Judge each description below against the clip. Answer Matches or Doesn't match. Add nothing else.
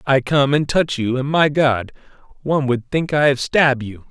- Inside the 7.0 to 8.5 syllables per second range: Doesn't match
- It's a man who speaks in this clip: Matches